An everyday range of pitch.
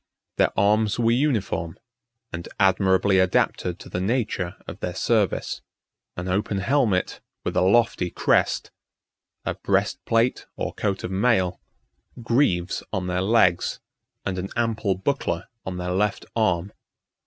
Yes: average, 3.9 semitones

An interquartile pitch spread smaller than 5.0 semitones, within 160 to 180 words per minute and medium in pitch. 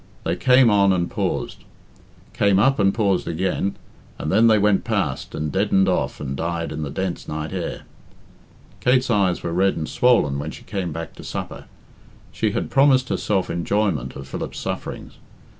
No: average, 4.2 semitones; average, 175 wpm; very low, 95 Hz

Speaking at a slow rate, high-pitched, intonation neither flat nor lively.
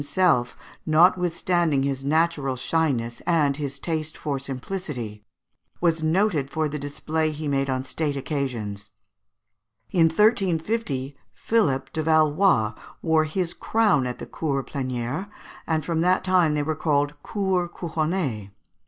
No: slow, 130 wpm; medium, 155 Hz; average, 3.9 semitones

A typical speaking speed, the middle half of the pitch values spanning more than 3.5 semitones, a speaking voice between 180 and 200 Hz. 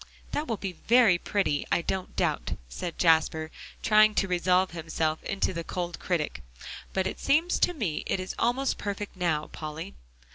Yes: average, 170 wpm; average, 4.4 semitones; medium, 185 Hz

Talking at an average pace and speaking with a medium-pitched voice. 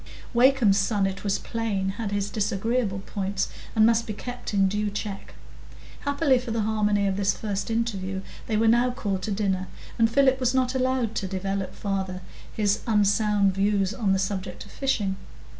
No: average, 175 wpm; high, 205 Hz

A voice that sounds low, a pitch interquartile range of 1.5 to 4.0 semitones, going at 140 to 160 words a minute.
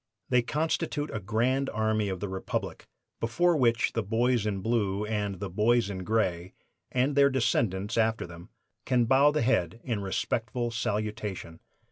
Yes: low, 110 Hz; average, 3.7 semitones; average, 155 wpm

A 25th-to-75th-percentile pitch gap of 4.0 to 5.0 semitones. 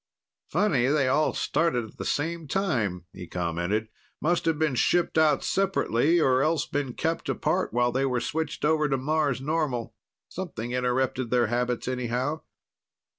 Yes: average, 4.5 semitones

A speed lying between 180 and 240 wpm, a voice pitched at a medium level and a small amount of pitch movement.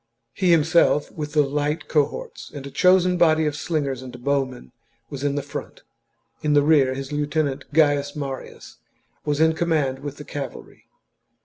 No: average, 165 wpm; medium, 145 Hz; narrow, 2.2 semitones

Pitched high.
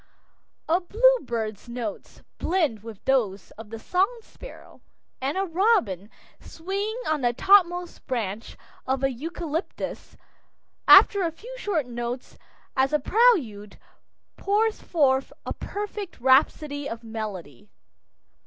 Yes: very high, 285 Hz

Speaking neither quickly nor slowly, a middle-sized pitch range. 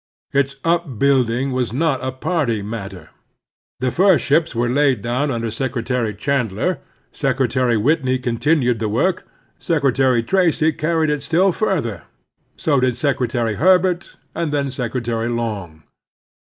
No: slow, 130 wpm; average, 4.6 semitones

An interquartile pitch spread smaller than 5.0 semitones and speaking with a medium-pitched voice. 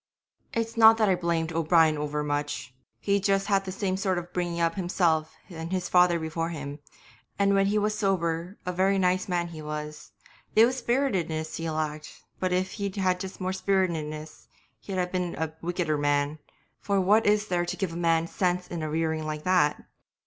Yes: average, 3.5 semitones; medium, 175 Hz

